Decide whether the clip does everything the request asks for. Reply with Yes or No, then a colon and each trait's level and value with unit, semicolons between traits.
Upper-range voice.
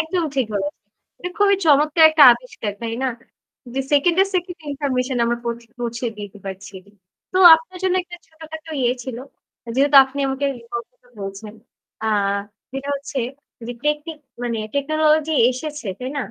Yes: very high, 280 Hz